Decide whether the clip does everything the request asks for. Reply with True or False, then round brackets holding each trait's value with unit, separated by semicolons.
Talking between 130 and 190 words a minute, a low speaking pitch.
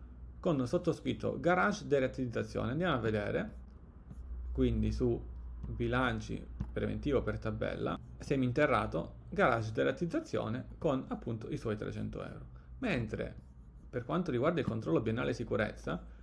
False (115 wpm; 110 Hz)